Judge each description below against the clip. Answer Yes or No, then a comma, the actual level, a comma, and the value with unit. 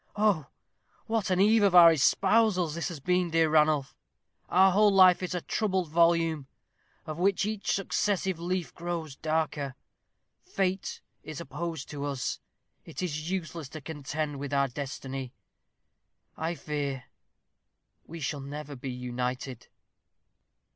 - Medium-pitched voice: Yes, medium, 160 Hz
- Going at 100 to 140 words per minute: Yes, slow, 135 wpm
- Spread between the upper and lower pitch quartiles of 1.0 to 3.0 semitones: No, average, 4.3 semitones